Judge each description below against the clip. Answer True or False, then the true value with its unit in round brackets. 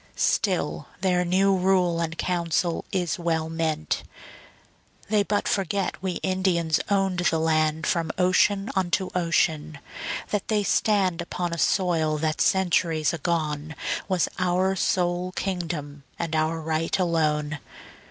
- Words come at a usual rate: False (125 wpm)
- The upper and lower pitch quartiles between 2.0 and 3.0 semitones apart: True (2.7 semitones)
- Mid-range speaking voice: True (175 Hz)